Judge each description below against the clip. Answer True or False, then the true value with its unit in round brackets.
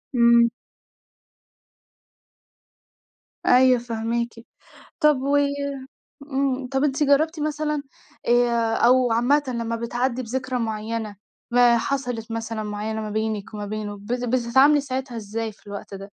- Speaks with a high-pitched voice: True (235 Hz)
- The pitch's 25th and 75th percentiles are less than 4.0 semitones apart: True (2.9 semitones)